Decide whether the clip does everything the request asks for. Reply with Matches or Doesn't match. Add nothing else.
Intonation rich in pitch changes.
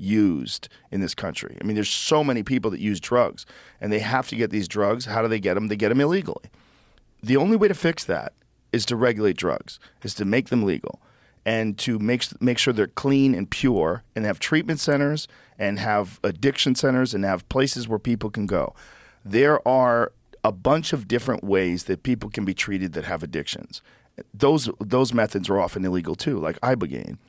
Doesn't match